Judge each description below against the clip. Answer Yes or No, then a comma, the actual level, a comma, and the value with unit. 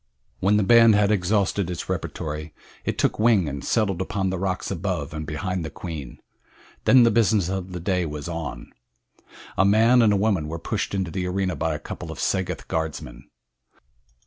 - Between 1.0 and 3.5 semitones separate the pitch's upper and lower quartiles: No, average, 3.9 semitones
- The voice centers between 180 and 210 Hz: No, very low, 95 Hz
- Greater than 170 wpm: Yes, average, 180 wpm